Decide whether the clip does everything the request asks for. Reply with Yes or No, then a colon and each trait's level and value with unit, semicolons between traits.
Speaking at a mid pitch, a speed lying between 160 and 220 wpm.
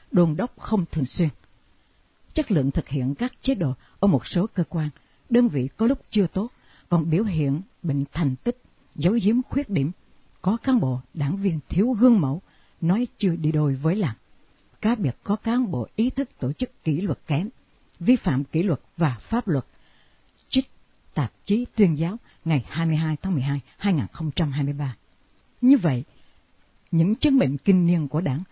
Yes: medium, 165 Hz; average, 180 wpm